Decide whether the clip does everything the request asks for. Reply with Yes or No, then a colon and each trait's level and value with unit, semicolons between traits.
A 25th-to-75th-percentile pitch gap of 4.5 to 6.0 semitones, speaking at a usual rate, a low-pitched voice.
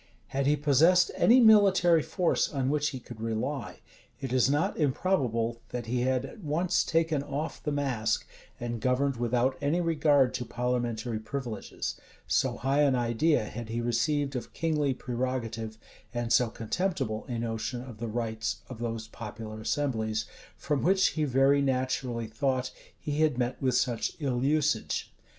No: average, 3.9 semitones; average, 160 wpm; low, 130 Hz